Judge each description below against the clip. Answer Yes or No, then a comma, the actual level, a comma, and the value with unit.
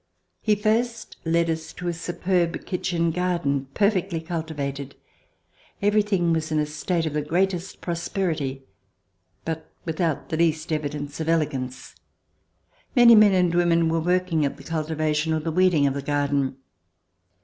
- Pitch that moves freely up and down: No, average, 3.0 semitones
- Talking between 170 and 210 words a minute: No, average, 150 wpm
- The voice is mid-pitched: Yes, medium, 165 Hz